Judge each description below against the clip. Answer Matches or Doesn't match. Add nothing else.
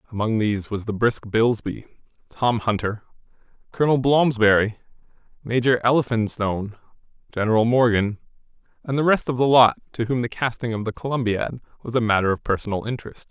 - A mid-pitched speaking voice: Doesn't match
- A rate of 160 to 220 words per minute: Doesn't match